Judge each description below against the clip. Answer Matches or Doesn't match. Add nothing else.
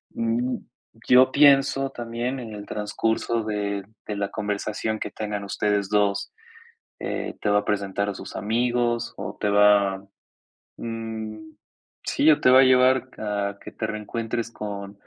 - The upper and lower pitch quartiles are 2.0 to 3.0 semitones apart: Matches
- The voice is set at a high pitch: Doesn't match